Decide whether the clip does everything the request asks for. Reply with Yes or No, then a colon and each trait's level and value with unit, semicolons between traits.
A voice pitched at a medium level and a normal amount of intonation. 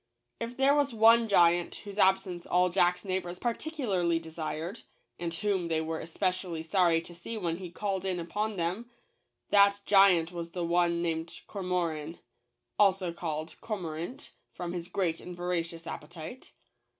Yes: medium, 180 Hz; average, 3.0 semitones